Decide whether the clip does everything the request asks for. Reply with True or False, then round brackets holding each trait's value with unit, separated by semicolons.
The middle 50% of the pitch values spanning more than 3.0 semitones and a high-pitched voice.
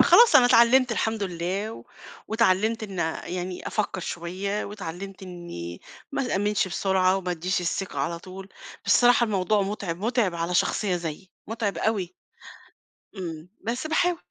True (3.8 semitones; 195 Hz)